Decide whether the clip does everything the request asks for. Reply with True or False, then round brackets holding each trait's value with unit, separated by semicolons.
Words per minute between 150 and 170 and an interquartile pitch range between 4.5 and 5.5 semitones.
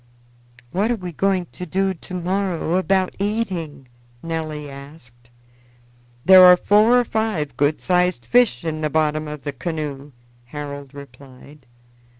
False (140 wpm; 4.8 semitones)